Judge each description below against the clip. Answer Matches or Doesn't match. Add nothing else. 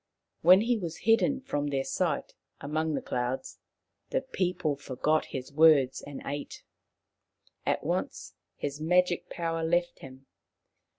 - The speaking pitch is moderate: Matches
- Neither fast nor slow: Doesn't match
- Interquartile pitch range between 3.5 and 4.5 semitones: Matches